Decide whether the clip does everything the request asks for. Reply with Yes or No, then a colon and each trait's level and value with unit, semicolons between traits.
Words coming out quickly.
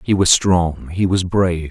Yes: fast, 210 wpm